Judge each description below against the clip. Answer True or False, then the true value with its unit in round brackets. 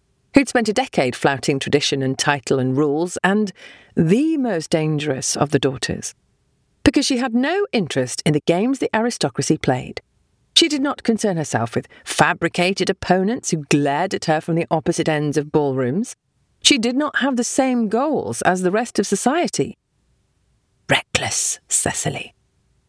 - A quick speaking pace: False (155 wpm)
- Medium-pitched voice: True (180 Hz)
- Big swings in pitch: True (8.2 semitones)